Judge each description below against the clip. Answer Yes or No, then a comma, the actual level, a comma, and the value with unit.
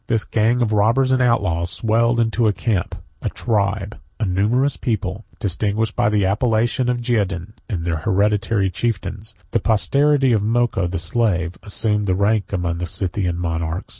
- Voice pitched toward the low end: Yes, low, 105 Hz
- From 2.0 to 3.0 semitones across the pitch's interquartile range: No, average, 3.8 semitones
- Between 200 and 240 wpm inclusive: No, average, 165 wpm